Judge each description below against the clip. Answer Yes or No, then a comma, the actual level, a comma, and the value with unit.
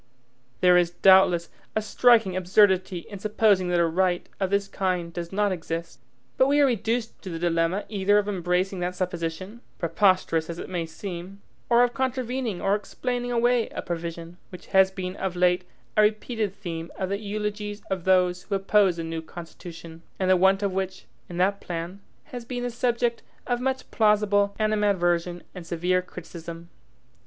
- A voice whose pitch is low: No, high, 190 Hz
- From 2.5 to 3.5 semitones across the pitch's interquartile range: Yes, average, 3.2 semitones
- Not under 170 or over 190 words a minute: Yes, average, 175 wpm